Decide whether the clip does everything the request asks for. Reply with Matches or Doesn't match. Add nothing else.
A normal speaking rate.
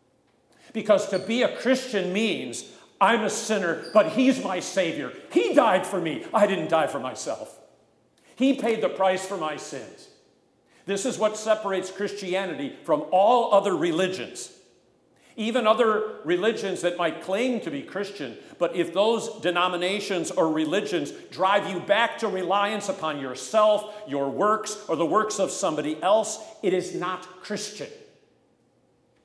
Matches